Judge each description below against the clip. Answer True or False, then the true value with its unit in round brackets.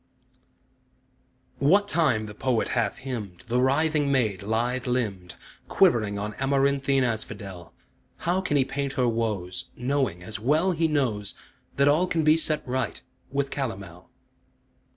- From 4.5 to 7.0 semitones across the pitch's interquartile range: True (4.8 semitones)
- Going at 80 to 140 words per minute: True (135 wpm)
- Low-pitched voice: True (130 Hz)